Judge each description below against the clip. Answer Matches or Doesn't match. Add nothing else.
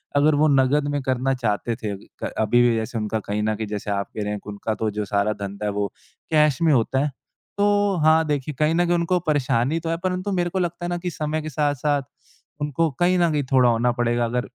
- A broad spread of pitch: Matches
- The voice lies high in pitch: Doesn't match